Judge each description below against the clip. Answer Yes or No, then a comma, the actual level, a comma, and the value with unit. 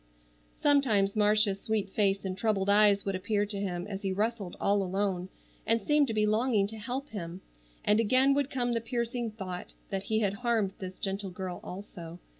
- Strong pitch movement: No, average, 2.8 semitones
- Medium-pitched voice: No, high, 205 Hz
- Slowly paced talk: No, average, 190 wpm